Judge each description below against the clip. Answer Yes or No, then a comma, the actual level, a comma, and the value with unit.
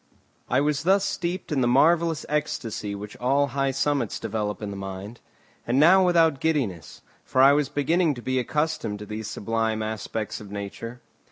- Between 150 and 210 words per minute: Yes, average, 175 wpm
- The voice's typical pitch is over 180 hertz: No, low, 130 Hz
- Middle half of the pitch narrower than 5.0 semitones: No, wide, 5.6 semitones